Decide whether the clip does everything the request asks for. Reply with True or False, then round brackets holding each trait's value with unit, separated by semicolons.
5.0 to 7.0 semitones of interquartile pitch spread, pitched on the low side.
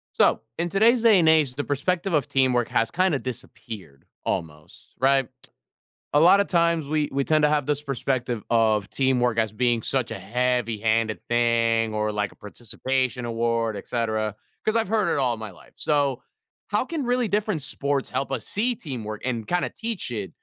True (5.5 semitones; 130 Hz)